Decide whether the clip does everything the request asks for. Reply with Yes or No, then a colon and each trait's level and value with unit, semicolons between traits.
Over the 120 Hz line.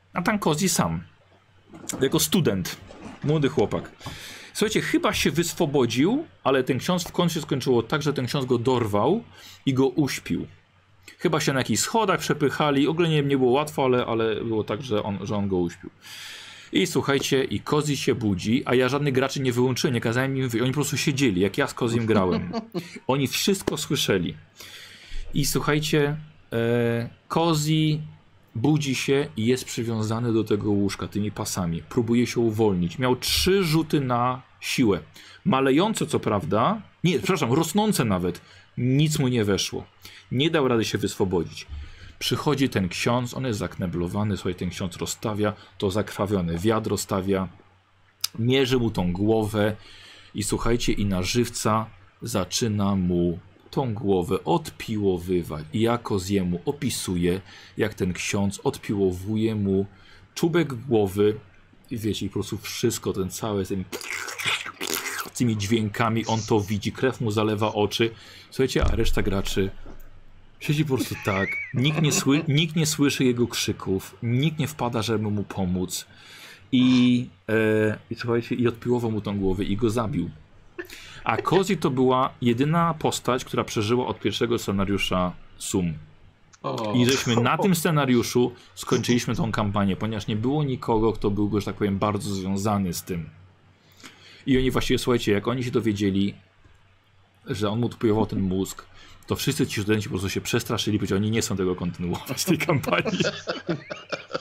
No: low, 110 Hz